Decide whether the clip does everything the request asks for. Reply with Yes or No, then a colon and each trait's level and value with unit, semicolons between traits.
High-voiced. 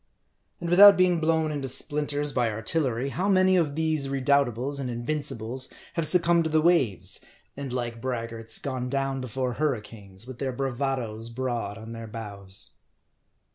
No: low, 135 Hz